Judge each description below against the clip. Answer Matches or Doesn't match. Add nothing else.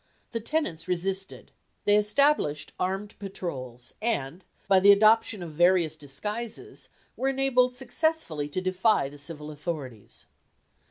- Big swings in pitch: Matches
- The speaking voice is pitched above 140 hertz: Matches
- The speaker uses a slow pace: Matches